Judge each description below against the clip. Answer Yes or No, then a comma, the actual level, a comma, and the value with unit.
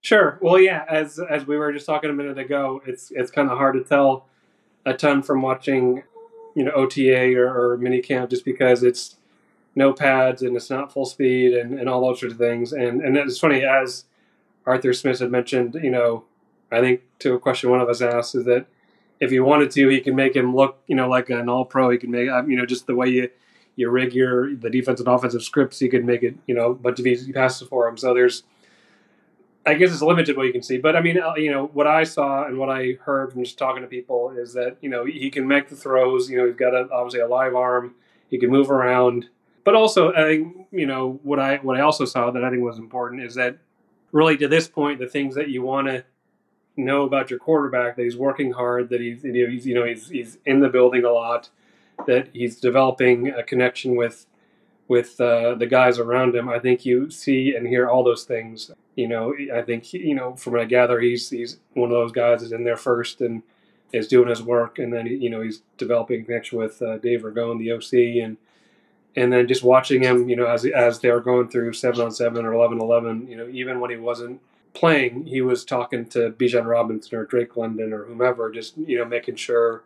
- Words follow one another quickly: Yes, fast, 235 wpm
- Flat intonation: Yes, narrow, 1.8 semitones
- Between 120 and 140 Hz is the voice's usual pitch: Yes, low, 125 Hz